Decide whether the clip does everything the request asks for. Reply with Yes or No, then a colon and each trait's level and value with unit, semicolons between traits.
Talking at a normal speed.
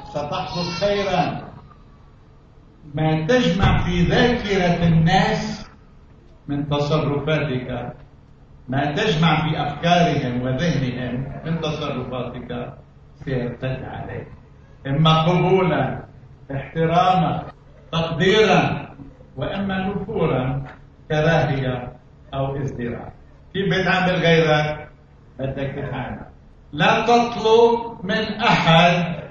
Yes: average, 75 wpm